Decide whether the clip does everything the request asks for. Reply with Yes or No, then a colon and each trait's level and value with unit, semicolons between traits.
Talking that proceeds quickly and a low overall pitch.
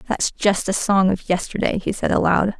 No: fast, 210 wpm; high, 195 Hz